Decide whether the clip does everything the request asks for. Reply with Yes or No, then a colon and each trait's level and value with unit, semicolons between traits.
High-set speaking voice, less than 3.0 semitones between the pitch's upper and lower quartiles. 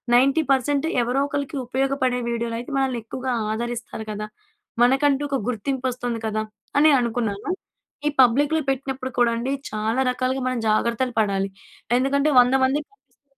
Yes: very high, 255 Hz; narrow, 2.6 semitones